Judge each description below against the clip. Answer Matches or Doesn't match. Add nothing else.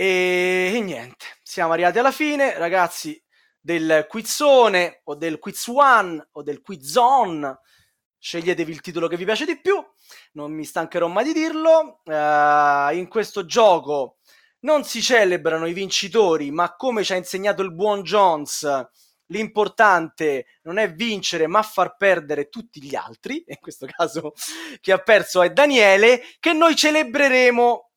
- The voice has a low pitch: Doesn't match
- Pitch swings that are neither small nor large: Doesn't match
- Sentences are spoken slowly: Doesn't match